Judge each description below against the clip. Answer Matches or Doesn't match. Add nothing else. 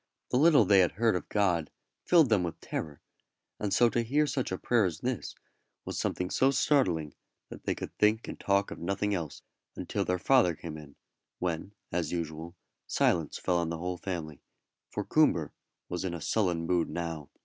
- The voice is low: Matches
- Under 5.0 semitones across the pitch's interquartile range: Matches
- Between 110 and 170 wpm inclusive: Doesn't match